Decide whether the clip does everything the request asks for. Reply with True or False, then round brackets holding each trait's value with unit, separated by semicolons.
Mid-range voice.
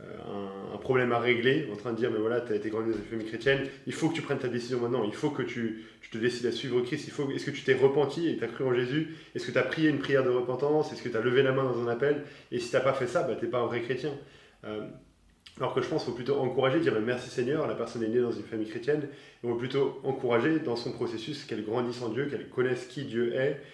False (125 Hz)